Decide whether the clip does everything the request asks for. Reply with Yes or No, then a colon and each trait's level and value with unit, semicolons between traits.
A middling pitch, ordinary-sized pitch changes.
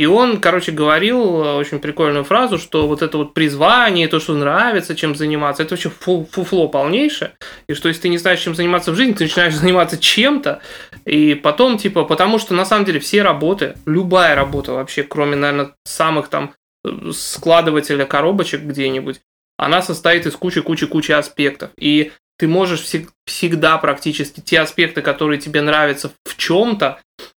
Yes: medium, 160 Hz; average, 3.2 semitones